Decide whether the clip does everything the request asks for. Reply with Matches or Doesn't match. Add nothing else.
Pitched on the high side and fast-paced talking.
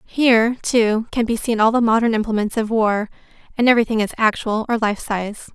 Doesn't match